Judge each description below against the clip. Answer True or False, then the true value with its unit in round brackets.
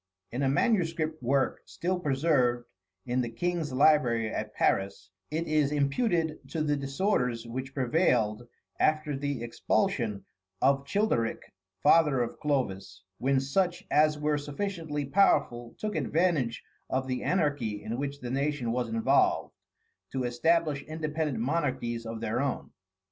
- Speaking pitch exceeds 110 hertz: True (140 Hz)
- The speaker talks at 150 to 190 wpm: False (135 wpm)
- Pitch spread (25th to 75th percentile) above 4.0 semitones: True (4.4 semitones)